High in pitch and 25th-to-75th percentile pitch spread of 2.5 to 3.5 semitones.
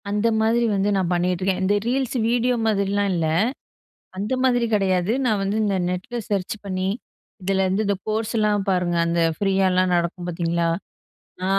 Yes: high, 195 Hz; average, 2.8 semitones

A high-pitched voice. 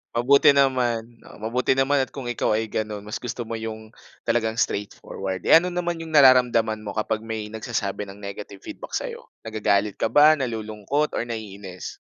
No: low, 115 Hz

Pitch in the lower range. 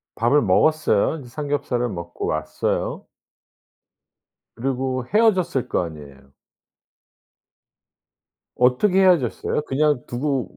Yes: low, 130 Hz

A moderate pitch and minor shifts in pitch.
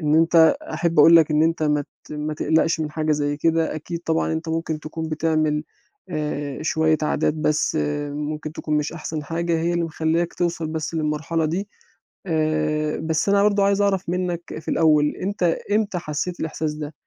Yes: medium, 160 Hz; narrow, 1.6 semitones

